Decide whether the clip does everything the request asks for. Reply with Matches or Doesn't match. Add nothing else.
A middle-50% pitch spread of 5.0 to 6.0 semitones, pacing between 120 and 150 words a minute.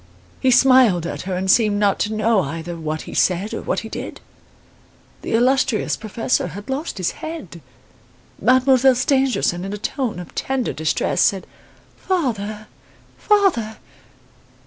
Matches